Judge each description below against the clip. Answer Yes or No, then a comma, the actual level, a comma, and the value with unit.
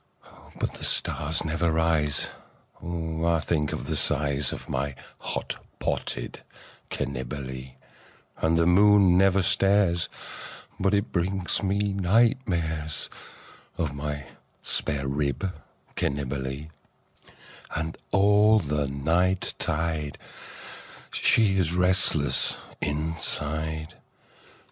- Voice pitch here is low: Yes, very low, 80 Hz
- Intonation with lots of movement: No, average, 4.2 semitones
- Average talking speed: No, slow, 100 wpm